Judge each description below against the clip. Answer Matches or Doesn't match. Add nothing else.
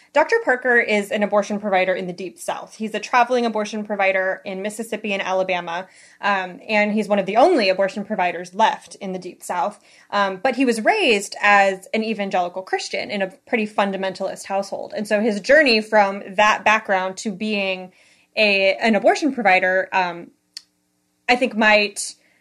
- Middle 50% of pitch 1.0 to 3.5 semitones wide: Matches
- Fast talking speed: Doesn't match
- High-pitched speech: Matches